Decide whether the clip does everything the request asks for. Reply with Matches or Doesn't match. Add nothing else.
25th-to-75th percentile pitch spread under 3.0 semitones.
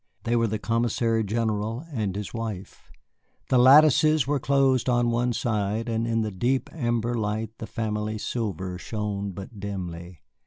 Matches